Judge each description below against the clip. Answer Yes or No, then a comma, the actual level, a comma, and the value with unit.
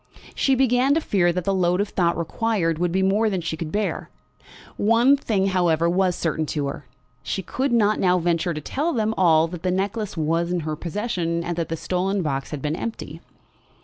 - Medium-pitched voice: Yes, medium, 180 Hz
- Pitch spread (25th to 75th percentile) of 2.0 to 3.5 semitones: No, average, 4.1 semitones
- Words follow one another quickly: Yes, fast, 210 wpm